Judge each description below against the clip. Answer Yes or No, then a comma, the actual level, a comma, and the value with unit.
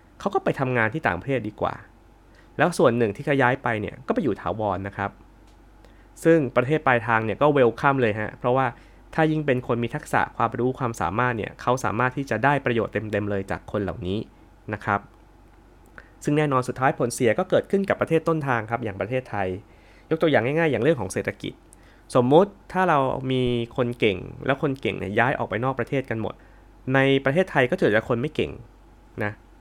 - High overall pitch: No, low, 115 Hz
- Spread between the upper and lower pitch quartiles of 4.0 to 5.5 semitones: Yes, average, 4.3 semitones